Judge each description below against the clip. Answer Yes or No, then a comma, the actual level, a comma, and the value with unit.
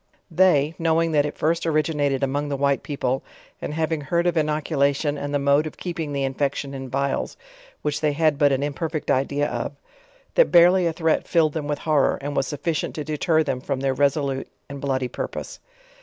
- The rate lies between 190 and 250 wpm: Yes, average, 200 wpm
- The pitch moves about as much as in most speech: No, narrow, 2.3 semitones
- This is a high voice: No, medium, 145 Hz